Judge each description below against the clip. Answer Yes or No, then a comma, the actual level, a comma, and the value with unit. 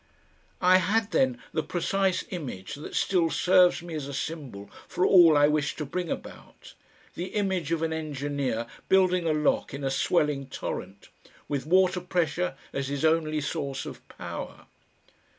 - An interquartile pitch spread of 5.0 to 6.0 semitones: No, average, 4.2 semitones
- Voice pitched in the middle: Yes, medium, 160 Hz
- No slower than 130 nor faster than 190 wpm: Yes, average, 160 wpm